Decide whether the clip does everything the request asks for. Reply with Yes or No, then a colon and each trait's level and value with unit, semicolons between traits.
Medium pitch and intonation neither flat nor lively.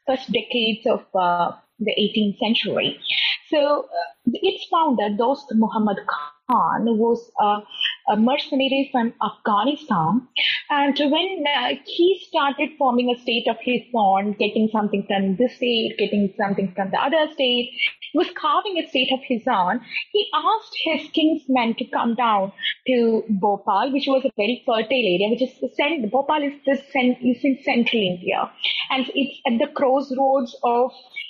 No: very high, 250 Hz; average, 4.4 semitones